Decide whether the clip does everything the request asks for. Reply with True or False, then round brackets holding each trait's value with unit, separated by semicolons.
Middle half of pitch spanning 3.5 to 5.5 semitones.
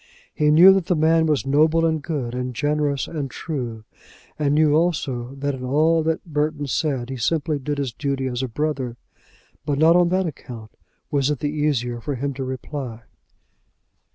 False (3.1 semitones)